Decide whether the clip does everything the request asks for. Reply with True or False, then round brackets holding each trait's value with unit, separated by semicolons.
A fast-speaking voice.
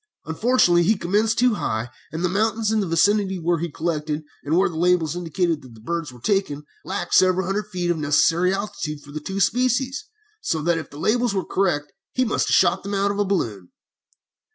True (220 wpm)